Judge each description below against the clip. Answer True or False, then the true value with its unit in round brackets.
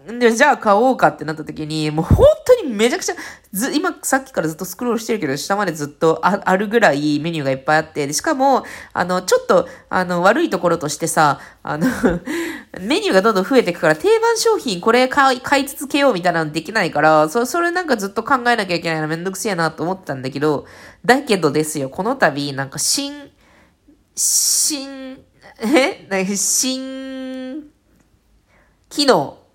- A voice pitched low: False (220 Hz)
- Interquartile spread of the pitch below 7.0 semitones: False (9.0 semitones)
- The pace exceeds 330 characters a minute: True (380 characters per minute)